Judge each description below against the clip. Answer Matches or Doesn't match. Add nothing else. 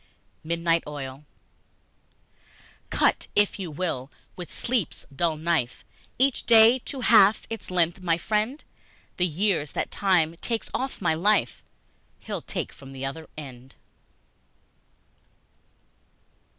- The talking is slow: Matches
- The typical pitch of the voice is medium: Matches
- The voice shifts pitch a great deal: Matches